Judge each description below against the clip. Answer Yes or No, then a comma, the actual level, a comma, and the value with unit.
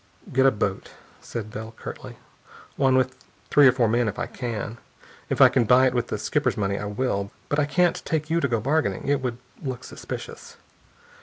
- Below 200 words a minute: No, fast, 205 wpm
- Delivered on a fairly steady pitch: No, average, 4.0 semitones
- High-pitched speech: No, low, 125 Hz